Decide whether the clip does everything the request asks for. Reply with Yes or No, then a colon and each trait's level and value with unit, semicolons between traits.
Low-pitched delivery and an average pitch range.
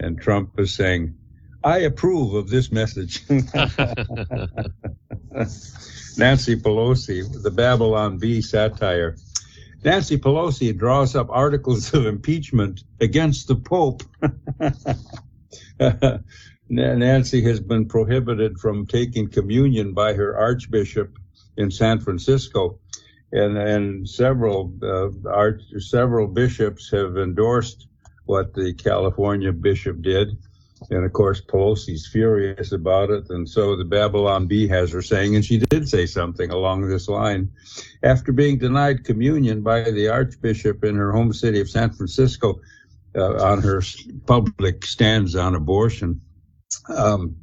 Yes: low, 110 Hz; average, 3.7 semitones